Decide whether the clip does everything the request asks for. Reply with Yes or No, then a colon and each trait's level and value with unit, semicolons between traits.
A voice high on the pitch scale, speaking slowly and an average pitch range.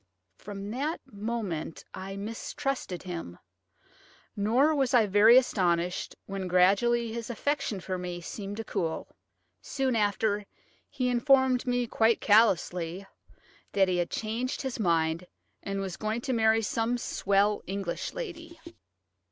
Yes: high, 215 Hz; slow, 130 wpm; average, 4.4 semitones